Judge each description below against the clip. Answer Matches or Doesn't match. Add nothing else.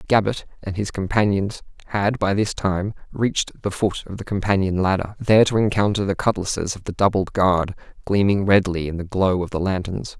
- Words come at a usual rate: Matches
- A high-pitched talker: Doesn't match